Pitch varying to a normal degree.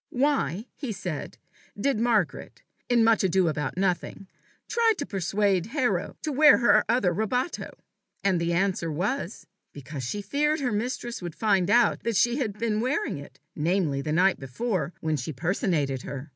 No: wide, 6.2 semitones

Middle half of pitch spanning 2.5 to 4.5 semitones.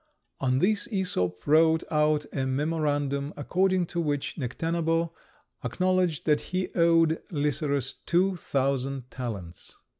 Yes: average, 3.6 semitones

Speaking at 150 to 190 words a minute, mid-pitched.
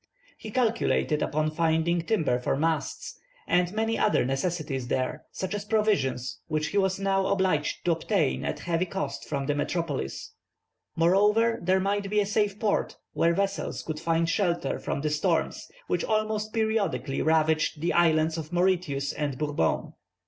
Yes: average, 155 wpm; medium, 170 Hz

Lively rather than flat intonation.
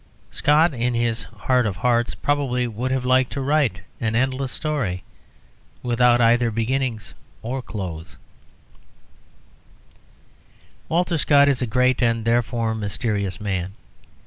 No: average, 2.8 semitones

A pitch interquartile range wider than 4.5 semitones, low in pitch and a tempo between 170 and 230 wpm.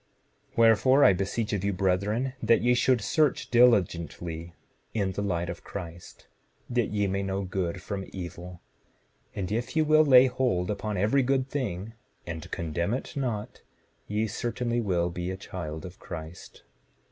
No: average, 5.2 semitones; low, 100 Hz; average, 160 wpm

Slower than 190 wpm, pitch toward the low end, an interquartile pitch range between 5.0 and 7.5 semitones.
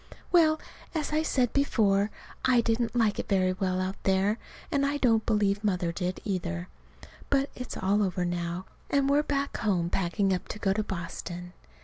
No: average, 175 wpm; high, 205 Hz; wide, 5.4 semitones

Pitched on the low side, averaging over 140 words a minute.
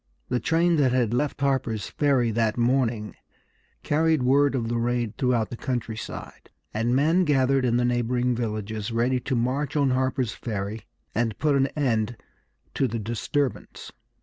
Yes: low, 125 Hz; average, 155 wpm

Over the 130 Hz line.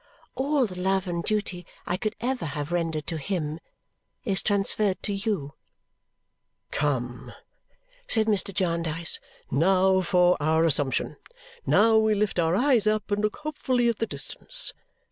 Yes: high, 190 Hz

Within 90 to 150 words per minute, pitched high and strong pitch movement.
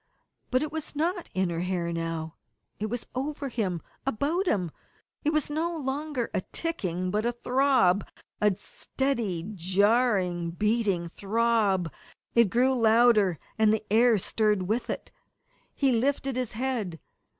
Yes: average, 140 wpm; high, 225 Hz; wide, 6.2 semitones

